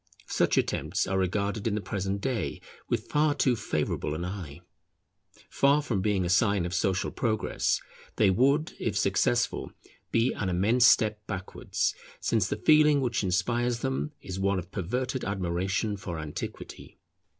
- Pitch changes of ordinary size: Yes, average, 4.7 semitones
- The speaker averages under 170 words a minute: Yes, average, 150 wpm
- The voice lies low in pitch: Yes, low, 100 Hz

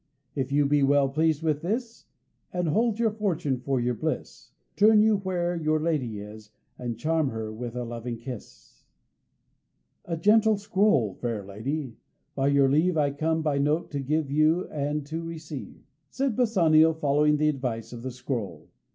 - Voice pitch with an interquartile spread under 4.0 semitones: No, average, 4.9 semitones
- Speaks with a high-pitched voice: No, medium, 150 Hz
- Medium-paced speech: Yes, average, 165 wpm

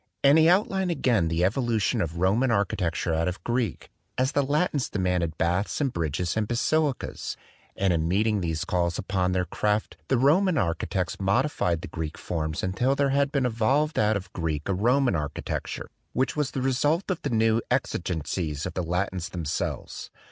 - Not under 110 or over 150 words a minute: No, average, 185 wpm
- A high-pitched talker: No, low, 100 Hz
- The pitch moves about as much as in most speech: No, wide, 7.4 semitones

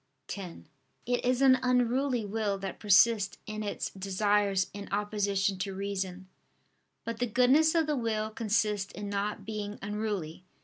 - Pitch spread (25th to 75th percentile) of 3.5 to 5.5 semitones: No, narrow, 2.6 semitones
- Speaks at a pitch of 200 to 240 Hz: Yes, high, 210 Hz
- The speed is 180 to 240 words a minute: No, average, 145 wpm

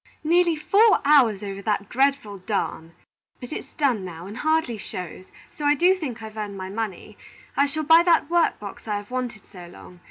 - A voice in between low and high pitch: No, high, 230 Hz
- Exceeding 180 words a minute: Yes, average, 195 wpm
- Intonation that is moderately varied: No, wide, 7.3 semitones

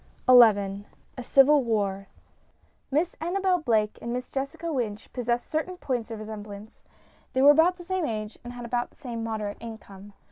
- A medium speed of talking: Yes, average, 170 wpm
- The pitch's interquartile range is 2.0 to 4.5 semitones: No, average, 5.3 semitones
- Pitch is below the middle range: No, high, 240 Hz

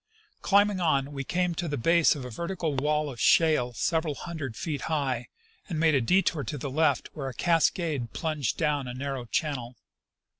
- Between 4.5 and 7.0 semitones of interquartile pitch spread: No, average, 3.8 semitones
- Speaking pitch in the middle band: Yes, medium, 150 Hz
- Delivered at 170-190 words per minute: Yes, average, 185 wpm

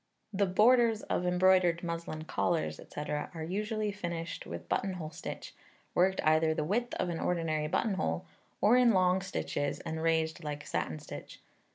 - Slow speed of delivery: No, average, 155 wpm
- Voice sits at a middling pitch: Yes, medium, 175 Hz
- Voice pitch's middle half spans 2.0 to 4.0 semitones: Yes, average, 3.5 semitones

